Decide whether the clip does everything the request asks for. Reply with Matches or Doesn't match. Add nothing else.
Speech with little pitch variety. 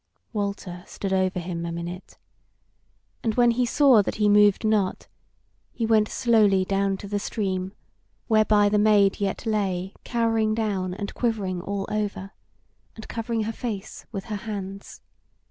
Matches